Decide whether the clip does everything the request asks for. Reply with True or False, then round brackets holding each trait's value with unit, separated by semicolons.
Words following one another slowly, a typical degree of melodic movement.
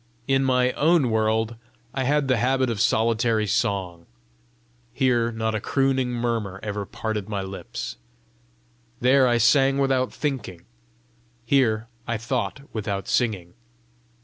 True (125 wpm; 3.4 semitones)